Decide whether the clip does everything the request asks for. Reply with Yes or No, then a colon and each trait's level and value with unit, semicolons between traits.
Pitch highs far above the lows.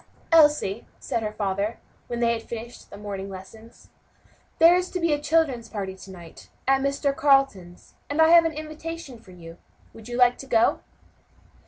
Yes: wide, 6.7 semitones